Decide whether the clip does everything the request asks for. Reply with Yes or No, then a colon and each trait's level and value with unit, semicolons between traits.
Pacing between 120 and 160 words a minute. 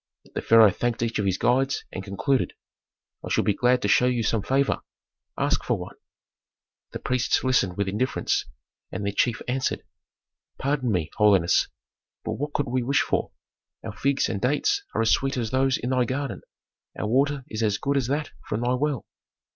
No: average, 185 wpm